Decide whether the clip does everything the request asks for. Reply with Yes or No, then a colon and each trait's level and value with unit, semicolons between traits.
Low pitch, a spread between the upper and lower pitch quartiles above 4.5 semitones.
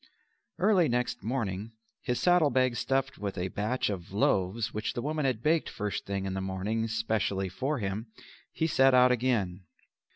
Yes: low, 115 Hz; average, 5.0 semitones